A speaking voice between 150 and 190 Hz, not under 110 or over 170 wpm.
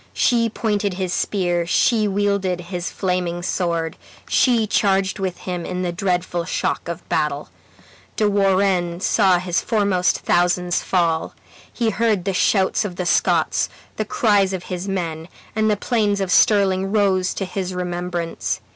Yes: medium, 185 Hz; average, 150 wpm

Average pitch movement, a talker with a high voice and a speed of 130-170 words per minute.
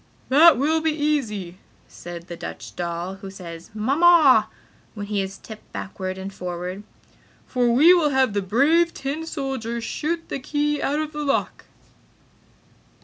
No: wide, 7.7 semitones; high, 245 Hz; average, 150 wpm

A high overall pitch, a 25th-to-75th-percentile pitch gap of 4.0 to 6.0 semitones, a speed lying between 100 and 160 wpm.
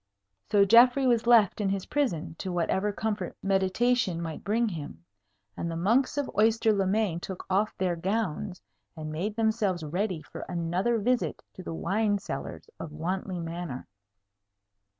Yes: high, 195 Hz; average, 4.3 semitones; average, 155 wpm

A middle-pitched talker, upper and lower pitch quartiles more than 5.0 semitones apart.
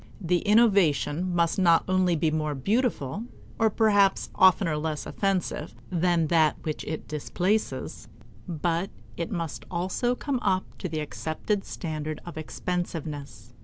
No: medium, 170 Hz; average, 3.8 semitones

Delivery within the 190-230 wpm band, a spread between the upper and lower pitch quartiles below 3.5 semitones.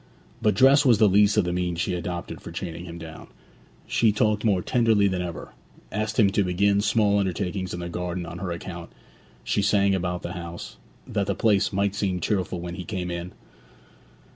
Yes: average, 195 wpm; average, 2.8 semitones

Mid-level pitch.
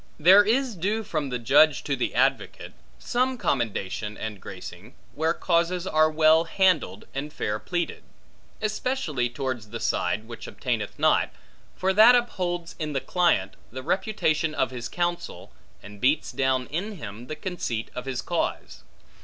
Yes: medium, 155 Hz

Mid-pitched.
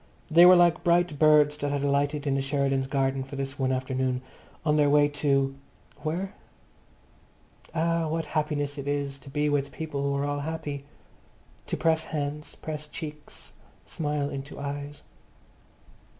Yes: medium, 145 Hz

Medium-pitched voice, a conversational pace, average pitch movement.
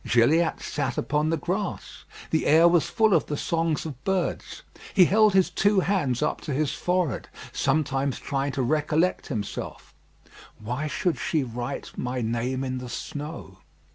Yes: medium, 150 Hz; average, 160 wpm; average, 4.8 semitones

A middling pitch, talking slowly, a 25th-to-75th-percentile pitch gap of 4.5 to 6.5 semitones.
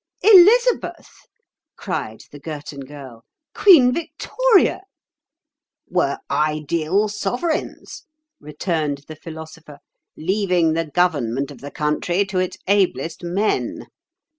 Yes: medium, 165 Hz; slow, 95 wpm; wide, 5.6 semitones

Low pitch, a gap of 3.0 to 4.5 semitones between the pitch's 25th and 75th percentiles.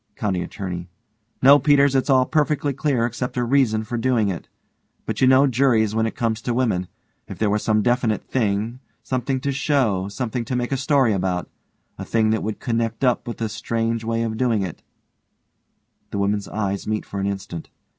Yes: low, 115 Hz; average, 3.5 semitones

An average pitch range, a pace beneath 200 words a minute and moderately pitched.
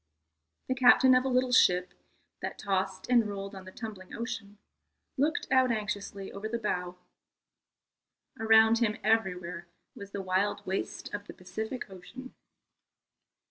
No: average, 3.8 semitones; average, 140 wpm; high, 210 Hz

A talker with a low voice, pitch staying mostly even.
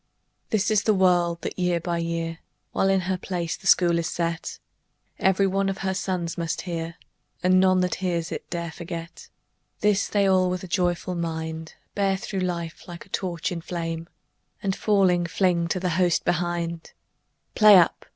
No: medium, 175 Hz; narrow, 2.0 semitones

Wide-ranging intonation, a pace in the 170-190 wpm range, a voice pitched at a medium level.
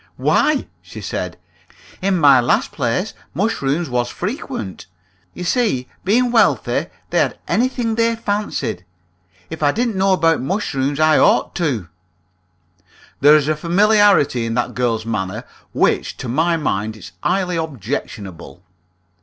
No: wide, 8.6 semitones; slow, 135 wpm; medium, 155 Hz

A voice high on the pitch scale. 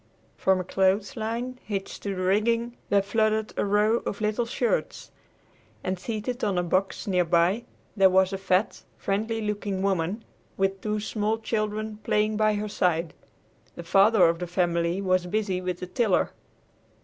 Yes: high, 200 Hz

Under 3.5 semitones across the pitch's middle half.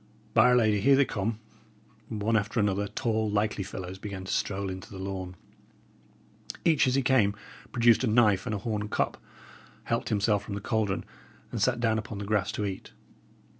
Yes: narrow, 2.5 semitones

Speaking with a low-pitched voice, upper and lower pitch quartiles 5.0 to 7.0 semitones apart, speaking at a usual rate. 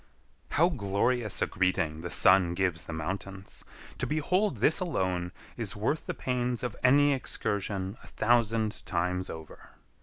Yes: low, 100 Hz; average, 5.3 semitones; average, 145 wpm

